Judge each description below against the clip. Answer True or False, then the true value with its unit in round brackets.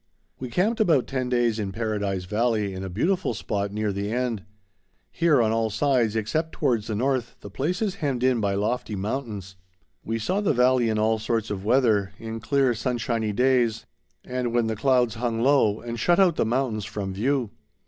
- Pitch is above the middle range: False (115 Hz)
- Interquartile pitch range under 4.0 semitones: True (3.5 semitones)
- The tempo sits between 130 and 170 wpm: False (190 wpm)